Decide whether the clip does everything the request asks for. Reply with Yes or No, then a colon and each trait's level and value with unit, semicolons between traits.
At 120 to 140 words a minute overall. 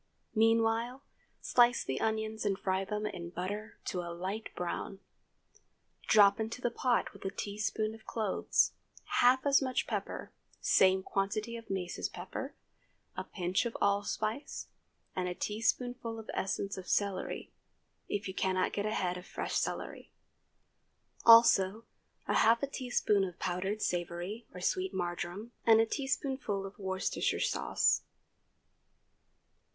Yes: slow, 135 wpm